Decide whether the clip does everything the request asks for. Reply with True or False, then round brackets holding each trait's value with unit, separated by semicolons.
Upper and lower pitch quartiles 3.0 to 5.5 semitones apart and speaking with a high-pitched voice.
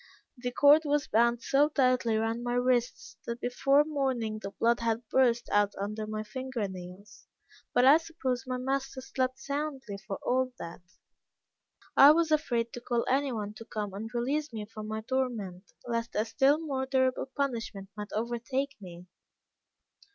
True (3.6 semitones; 245 Hz)